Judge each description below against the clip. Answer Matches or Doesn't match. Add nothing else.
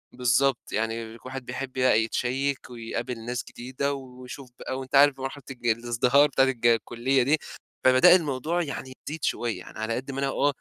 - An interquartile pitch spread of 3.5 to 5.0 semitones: Doesn't match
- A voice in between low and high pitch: Doesn't match